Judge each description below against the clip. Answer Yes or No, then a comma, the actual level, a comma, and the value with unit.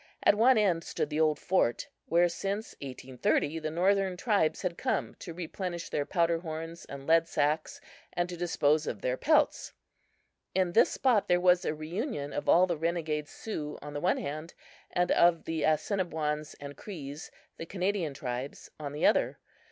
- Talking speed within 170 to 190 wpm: Yes, average, 175 wpm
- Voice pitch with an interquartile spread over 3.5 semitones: No, average, 3.2 semitones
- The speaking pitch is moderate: Yes, medium, 165 Hz